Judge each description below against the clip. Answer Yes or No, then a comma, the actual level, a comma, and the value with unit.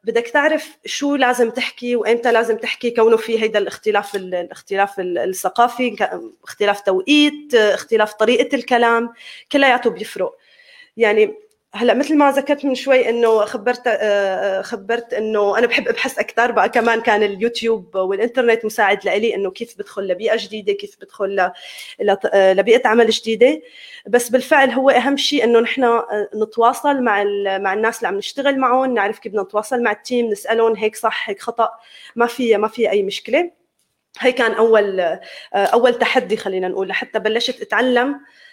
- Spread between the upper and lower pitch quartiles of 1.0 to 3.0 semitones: No, average, 3.6 semitones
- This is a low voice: No, high, 235 Hz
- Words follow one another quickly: Yes, fast, 150 wpm